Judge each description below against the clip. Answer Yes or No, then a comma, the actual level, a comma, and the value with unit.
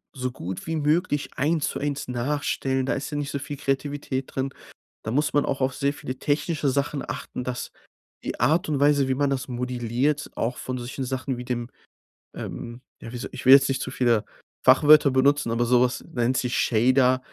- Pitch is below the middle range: Yes, low, 130 Hz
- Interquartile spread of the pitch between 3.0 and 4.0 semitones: No, narrow, 2.5 semitones